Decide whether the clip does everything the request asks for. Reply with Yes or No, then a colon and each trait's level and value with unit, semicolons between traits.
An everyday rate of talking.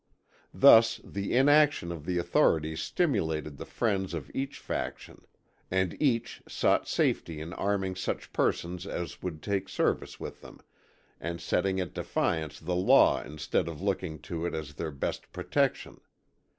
Yes: average, 150 wpm